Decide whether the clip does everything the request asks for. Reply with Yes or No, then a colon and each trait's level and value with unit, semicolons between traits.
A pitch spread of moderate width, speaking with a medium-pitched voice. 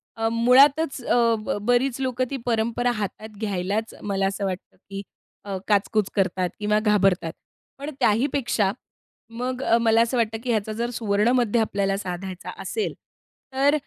No: average, 3.5 semitones; high, 220 Hz